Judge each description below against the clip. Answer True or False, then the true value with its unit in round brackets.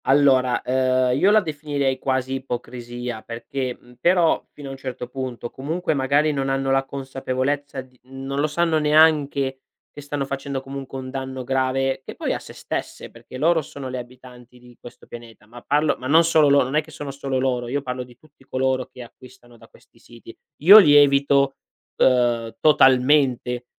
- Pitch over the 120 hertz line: True (135 Hz)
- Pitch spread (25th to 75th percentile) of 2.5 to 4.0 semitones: False (2.1 semitones)